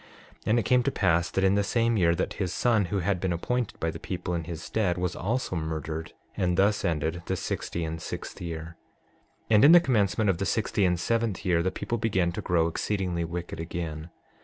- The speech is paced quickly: Yes, fast, 220 wpm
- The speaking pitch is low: Yes, very low, 90 Hz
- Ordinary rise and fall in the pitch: Yes, average, 3.6 semitones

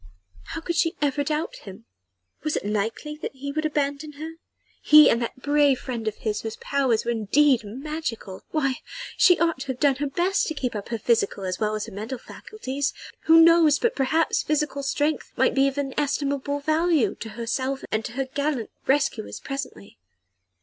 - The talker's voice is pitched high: Yes, very high, 275 Hz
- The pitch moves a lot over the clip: No, average, 4.5 semitones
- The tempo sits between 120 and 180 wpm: No, average, 190 wpm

